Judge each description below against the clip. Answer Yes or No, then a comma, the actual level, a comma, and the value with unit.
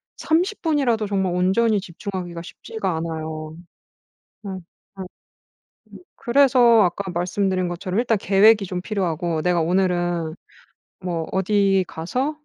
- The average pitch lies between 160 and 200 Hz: Yes, high, 190 Hz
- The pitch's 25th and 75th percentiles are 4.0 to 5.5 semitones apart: No, average, 3.6 semitones